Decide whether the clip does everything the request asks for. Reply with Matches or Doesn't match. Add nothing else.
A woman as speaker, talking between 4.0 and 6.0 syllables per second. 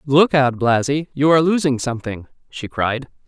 Matches